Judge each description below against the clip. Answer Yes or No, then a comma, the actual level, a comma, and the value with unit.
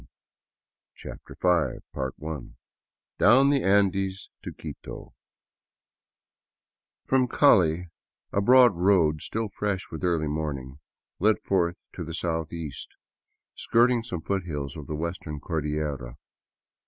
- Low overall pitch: Yes, very low, 85 Hz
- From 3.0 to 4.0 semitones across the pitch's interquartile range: No, average, 4.5 semitones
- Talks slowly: Yes, slow, 110 wpm